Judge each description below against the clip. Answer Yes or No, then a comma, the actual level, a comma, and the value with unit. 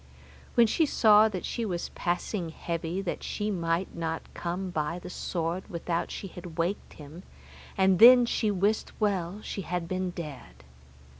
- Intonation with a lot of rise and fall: No, average, 3.4 semitones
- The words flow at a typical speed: Yes, average, 160 wpm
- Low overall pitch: No, medium, 180 Hz